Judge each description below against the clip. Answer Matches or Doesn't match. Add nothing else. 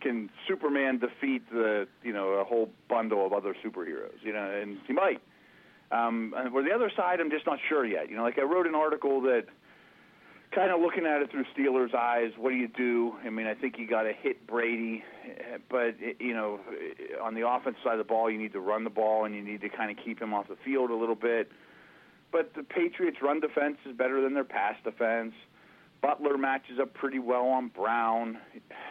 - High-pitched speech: Doesn't match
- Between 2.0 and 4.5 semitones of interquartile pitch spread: Matches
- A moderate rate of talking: Doesn't match